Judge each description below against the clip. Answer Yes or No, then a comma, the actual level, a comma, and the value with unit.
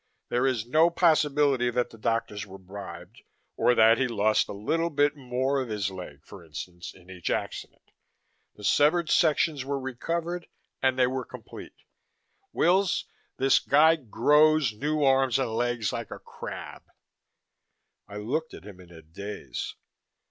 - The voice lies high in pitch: No, low, 125 Hz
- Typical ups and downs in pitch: No, wide, 6.2 semitones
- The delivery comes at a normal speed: Yes, average, 155 wpm